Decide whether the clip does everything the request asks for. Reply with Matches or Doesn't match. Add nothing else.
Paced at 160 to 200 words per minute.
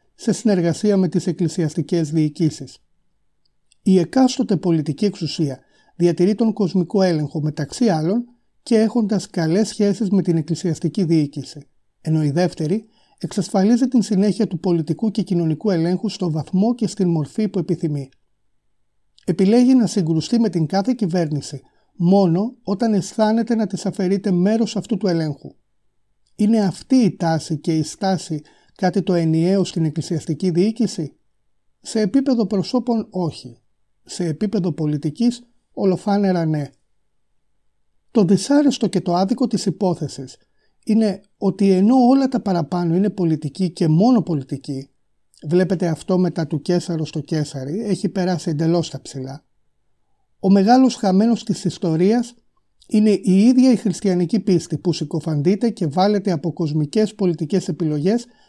Doesn't match